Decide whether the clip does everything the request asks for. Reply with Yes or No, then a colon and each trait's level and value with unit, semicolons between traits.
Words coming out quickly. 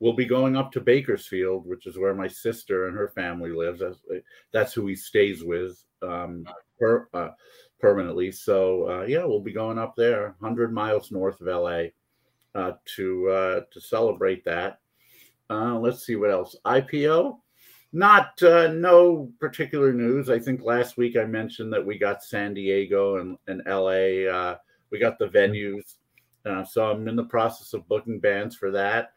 No: average, 175 wpm